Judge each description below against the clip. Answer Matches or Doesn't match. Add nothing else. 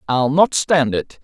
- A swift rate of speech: Doesn't match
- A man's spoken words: Matches